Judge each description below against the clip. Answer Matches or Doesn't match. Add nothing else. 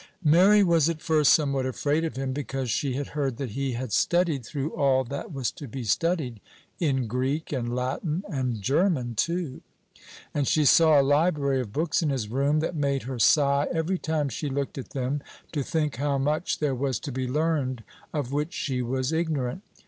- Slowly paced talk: Doesn't match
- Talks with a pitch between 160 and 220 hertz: Doesn't match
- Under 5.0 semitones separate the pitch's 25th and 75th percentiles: Matches